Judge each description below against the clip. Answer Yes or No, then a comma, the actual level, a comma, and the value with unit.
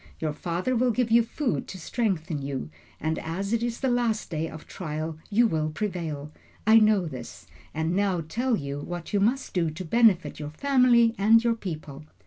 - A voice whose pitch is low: No, medium, 185 Hz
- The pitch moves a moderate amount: No, wide, 6.6 semitones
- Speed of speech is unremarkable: Yes, average, 190 wpm